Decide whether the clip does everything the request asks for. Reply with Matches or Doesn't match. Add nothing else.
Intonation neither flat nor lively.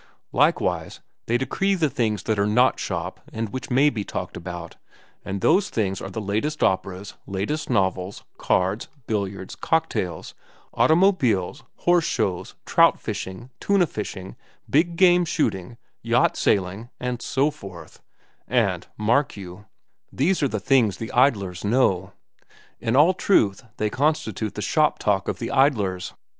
Doesn't match